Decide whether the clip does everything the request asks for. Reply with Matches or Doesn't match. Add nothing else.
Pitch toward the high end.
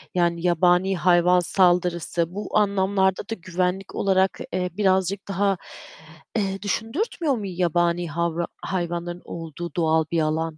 Doesn't match